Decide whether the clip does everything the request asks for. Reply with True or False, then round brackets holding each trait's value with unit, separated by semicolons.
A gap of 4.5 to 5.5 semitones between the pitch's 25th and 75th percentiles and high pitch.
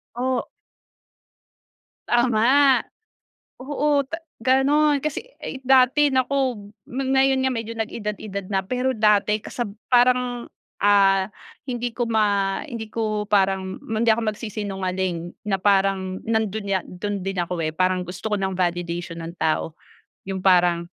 True (4.8 semitones; 210 Hz)